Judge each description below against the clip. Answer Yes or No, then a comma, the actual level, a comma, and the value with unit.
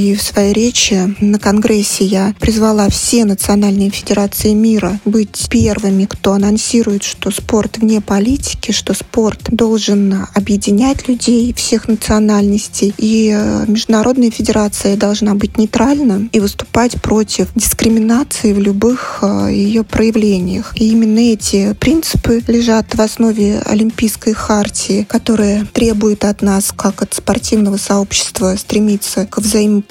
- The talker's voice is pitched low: No, high, 215 Hz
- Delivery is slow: No, average, 120 wpm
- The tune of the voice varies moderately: No, narrow, 1.8 semitones